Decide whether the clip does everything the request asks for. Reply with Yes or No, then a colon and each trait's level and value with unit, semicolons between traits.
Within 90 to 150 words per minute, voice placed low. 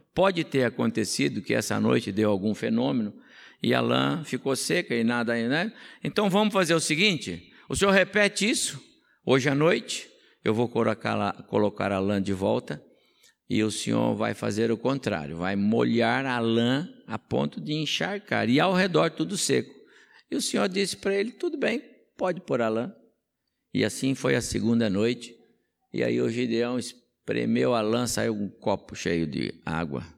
No: average, 175 wpm; low, 120 Hz